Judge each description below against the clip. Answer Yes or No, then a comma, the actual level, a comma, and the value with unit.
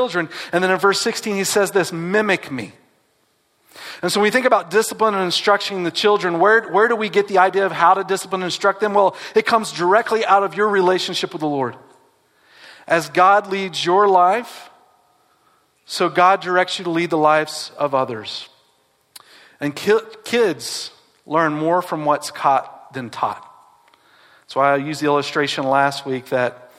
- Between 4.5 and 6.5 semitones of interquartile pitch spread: Yes, average, 4.8 semitones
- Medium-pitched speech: Yes, medium, 180 Hz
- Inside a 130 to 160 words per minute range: No, average, 180 wpm